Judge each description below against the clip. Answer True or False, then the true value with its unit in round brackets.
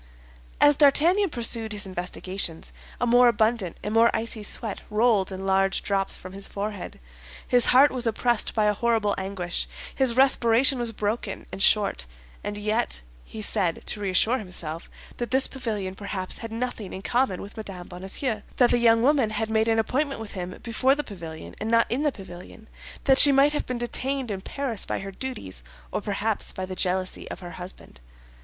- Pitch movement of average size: True (4.1 semitones)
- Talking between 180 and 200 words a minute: True (185 wpm)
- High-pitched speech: True (220 Hz)